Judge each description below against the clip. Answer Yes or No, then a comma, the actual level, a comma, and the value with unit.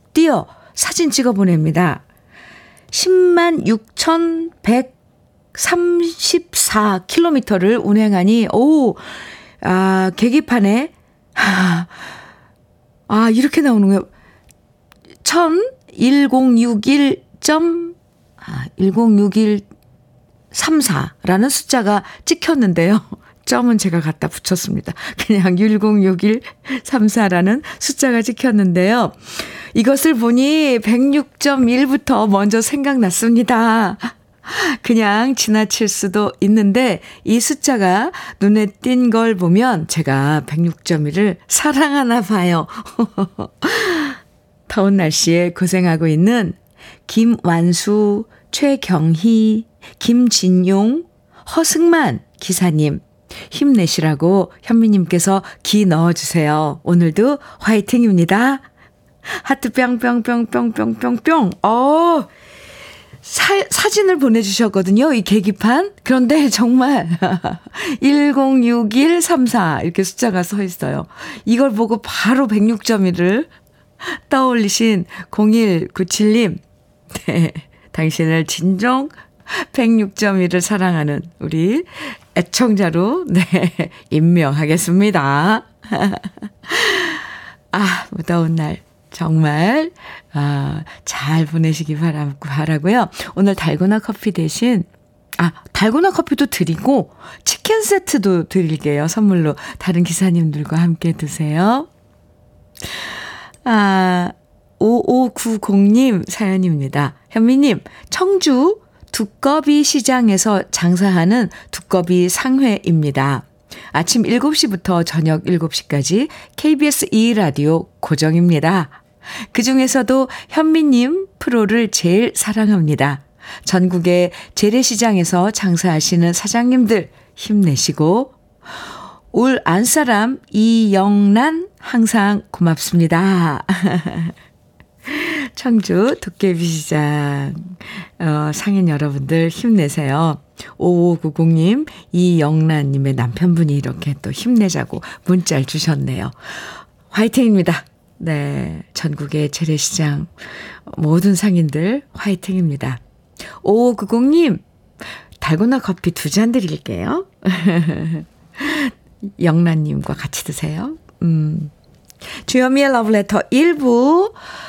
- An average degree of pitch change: No, wide, 6.7 semitones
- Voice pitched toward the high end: Yes, high, 205 Hz